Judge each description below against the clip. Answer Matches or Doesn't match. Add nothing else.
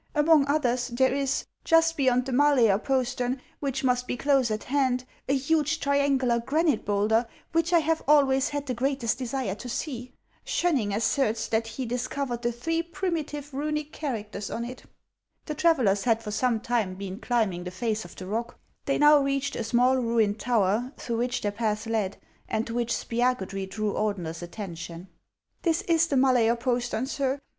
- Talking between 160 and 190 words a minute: Matches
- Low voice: Doesn't match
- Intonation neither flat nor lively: Matches